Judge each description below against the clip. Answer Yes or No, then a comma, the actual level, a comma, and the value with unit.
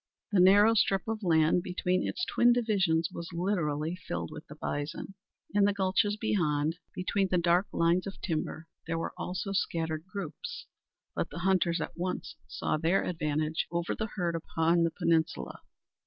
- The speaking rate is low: No, average, 165 wpm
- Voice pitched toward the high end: No, medium, 175 Hz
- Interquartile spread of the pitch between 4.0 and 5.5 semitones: No, average, 3.3 semitones